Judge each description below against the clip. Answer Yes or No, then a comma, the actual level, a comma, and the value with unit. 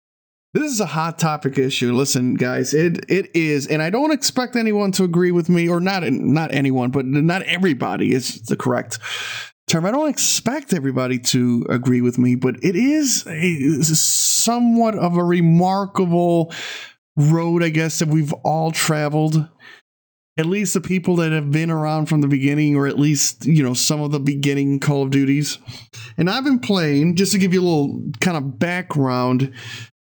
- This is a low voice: No, medium, 155 Hz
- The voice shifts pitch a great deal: No, average, 4.9 semitones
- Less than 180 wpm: No, average, 185 wpm